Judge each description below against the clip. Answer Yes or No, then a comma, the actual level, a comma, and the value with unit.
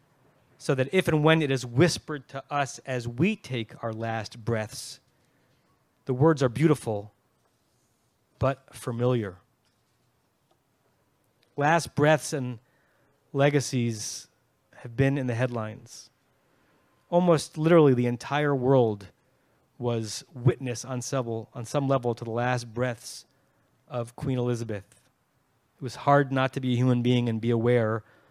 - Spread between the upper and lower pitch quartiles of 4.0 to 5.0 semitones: No, average, 2.7 semitones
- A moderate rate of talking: No, slow, 130 wpm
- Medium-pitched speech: No, low, 130 Hz